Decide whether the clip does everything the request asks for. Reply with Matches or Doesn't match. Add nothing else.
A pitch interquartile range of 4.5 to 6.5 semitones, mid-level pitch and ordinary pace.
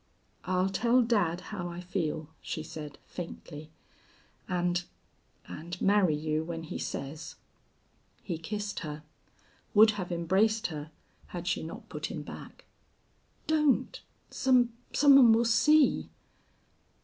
Doesn't match